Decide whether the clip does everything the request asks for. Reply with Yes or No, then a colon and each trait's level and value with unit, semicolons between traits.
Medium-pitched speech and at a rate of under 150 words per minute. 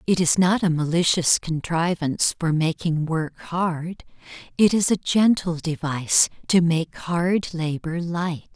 Yes: medium, 170 Hz; average, 140 wpm